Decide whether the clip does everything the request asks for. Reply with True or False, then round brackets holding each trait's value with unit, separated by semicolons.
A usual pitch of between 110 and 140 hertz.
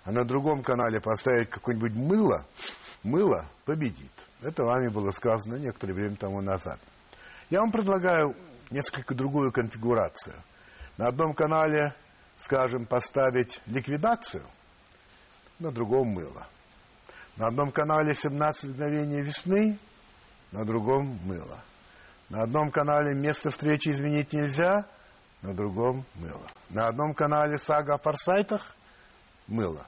True (135 Hz)